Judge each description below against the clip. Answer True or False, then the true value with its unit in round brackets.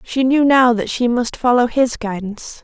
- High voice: True (240 Hz)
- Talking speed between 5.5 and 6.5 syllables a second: False (4.7 syllables/s)